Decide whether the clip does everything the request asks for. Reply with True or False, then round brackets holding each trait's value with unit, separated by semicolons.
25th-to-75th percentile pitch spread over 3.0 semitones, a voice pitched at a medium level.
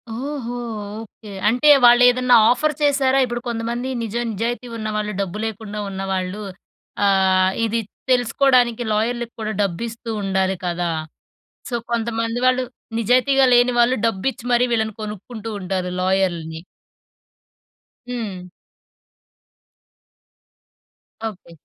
False (4.0 semitones; 225 Hz)